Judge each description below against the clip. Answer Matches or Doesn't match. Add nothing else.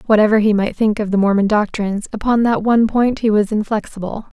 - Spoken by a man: Doesn't match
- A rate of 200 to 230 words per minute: Matches